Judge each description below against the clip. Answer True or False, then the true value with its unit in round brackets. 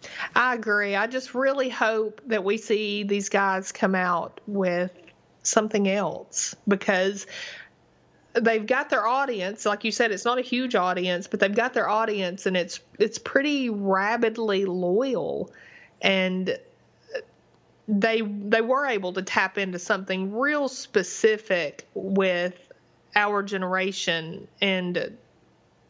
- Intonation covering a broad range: False (3.5 semitones)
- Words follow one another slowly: True (125 wpm)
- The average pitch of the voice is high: True (205 Hz)